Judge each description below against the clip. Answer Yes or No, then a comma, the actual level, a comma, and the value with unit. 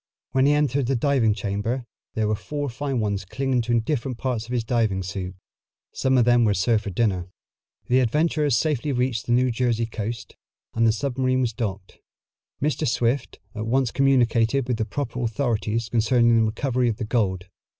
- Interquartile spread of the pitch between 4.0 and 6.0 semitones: No, average, 3.1 semitones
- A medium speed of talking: Yes, average, 180 wpm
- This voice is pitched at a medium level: No, low, 120 Hz